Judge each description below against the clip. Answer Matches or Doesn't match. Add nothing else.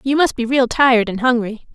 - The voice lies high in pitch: Matches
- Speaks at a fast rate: Matches